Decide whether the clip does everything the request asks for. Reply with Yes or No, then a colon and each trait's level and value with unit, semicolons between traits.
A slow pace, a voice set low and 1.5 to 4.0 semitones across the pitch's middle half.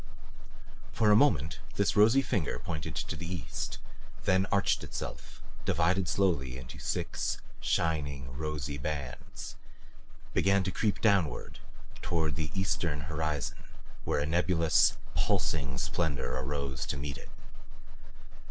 No: slow, 120 wpm; very low, 80 Hz; average, 4.8 semitones